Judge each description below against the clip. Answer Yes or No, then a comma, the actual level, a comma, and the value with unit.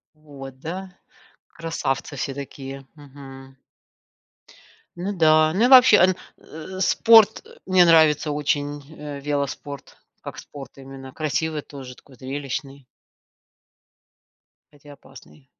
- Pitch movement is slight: No, average, 3.1 semitones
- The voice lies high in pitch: No, medium, 145 Hz